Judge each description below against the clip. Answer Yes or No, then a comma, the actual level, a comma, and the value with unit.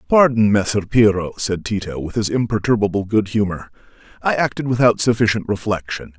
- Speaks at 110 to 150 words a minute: Yes, average, 145 wpm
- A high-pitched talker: No, low, 110 Hz